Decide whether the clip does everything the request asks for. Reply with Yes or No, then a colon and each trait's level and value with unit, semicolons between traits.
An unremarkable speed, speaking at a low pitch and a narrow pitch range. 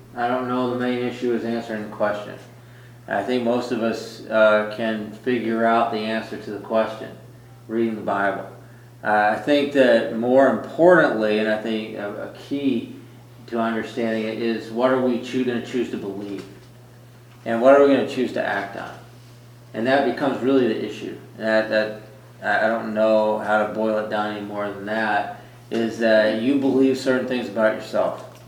Yes: average, 190 wpm; low, 115 Hz; narrow, 2.3 semitones